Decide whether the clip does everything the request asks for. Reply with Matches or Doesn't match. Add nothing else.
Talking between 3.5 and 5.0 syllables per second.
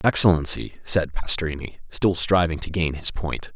Doesn't match